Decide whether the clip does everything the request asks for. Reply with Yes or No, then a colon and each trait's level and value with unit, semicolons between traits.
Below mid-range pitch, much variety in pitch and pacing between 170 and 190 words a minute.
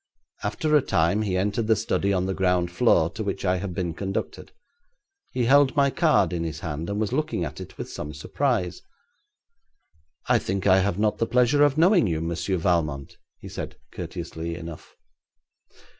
Yes: very low, 95 Hz; wide, 5.7 semitones; average, 180 wpm